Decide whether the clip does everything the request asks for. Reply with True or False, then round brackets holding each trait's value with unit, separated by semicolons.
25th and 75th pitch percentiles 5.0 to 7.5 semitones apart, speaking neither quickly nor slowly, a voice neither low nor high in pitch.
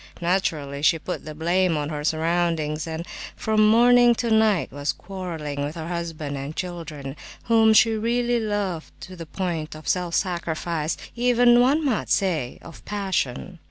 True (5.6 semitones; 160 wpm; 175 Hz)